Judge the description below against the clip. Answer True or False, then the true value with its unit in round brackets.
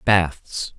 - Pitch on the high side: False (90 Hz)